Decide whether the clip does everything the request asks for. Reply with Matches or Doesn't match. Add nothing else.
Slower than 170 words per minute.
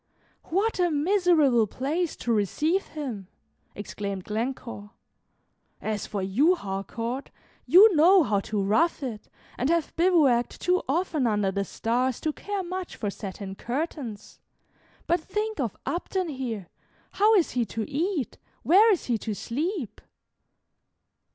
Matches